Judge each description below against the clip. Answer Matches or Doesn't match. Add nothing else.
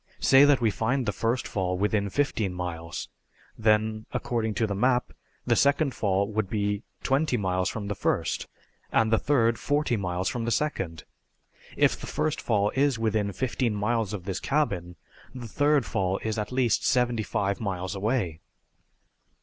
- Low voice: Matches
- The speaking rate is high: Doesn't match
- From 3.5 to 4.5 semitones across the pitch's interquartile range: Matches